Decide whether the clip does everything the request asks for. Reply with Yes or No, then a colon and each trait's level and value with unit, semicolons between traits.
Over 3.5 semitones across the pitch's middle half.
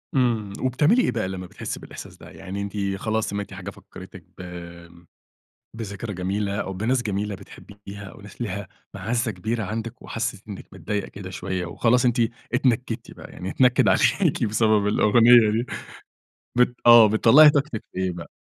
No: average, 3.2 semitones